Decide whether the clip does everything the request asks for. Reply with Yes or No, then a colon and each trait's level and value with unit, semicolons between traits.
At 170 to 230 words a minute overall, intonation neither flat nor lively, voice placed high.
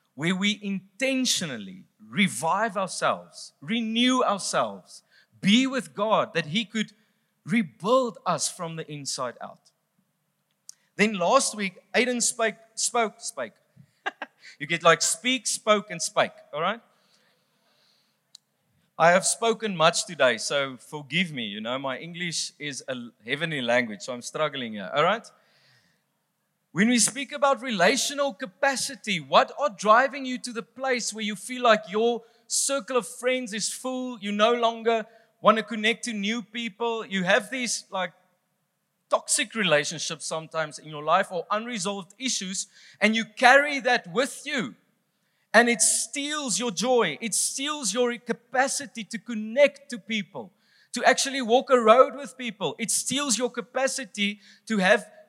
No: average, 145 wpm; average, 4.9 semitones; high, 220 Hz